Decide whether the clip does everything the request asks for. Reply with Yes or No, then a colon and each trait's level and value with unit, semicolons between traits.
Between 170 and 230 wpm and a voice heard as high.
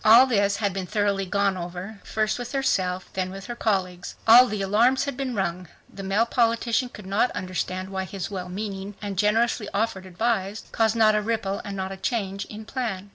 Yes: average, 195 wpm; high, 200 Hz